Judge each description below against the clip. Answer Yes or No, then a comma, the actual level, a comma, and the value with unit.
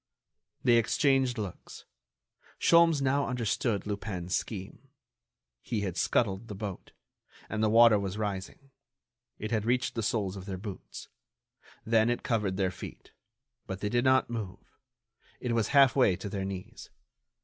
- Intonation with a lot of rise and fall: No, average, 3.8 semitones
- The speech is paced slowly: No, average, 150 wpm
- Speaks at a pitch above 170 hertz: No, low, 110 Hz